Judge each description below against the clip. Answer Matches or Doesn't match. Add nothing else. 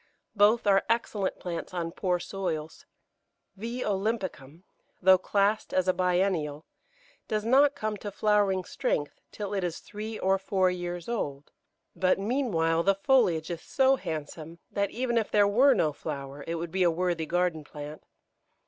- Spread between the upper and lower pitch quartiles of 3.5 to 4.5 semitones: Matches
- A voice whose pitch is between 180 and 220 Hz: Matches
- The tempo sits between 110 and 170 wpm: Matches